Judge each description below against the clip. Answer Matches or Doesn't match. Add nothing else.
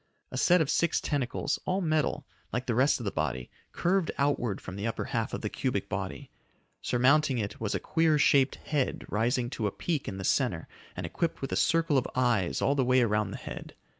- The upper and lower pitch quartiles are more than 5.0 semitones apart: Matches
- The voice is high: Doesn't match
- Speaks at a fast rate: Matches